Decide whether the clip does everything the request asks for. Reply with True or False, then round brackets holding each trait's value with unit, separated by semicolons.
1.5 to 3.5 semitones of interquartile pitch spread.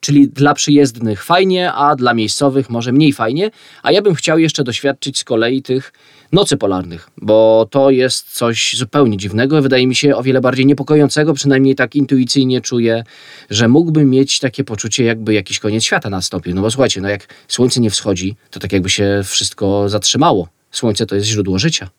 False (4.8 semitones)